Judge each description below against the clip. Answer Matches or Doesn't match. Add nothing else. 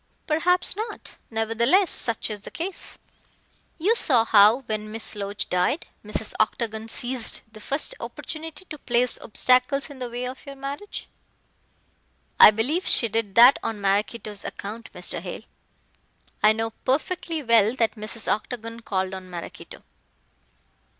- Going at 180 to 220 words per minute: Doesn't match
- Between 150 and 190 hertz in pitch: Doesn't match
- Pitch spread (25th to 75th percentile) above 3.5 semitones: Matches